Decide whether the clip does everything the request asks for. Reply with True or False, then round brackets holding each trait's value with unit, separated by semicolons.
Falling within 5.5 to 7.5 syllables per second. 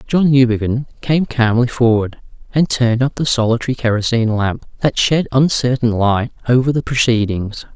False (5.2 syllables/s)